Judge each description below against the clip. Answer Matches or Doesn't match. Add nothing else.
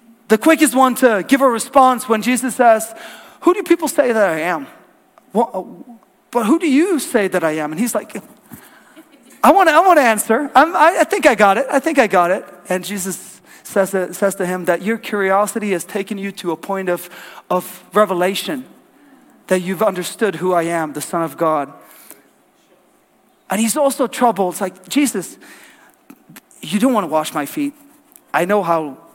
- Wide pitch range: Matches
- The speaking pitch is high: Matches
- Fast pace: Doesn't match